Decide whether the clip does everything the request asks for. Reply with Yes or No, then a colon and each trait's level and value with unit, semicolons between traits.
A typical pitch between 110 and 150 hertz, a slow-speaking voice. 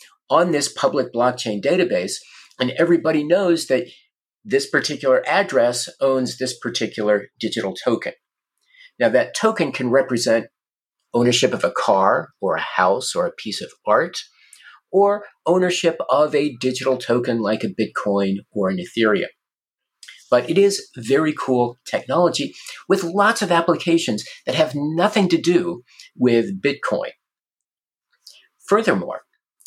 Yes: medium, 140 Hz; slow, 130 wpm